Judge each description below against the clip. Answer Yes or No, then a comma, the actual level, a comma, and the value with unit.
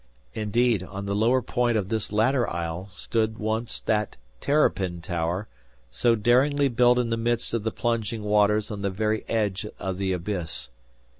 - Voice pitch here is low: Yes, low, 110 Hz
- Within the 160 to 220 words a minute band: Yes, average, 165 wpm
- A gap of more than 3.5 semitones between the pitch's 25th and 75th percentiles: No, average, 3.1 semitones